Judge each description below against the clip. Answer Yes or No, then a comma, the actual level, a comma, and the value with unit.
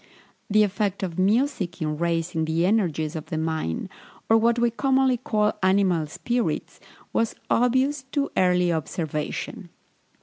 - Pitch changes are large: Yes, wide, 6.3 semitones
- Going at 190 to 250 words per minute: No, slow, 135 wpm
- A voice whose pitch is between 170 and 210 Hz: Yes, high, 190 Hz